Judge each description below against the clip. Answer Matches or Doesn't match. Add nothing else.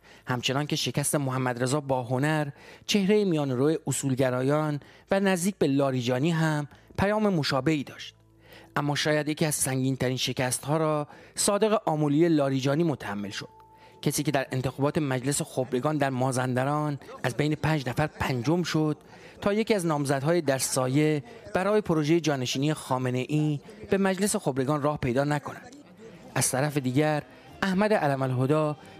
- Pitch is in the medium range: Matches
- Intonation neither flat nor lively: Matches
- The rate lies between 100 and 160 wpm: Matches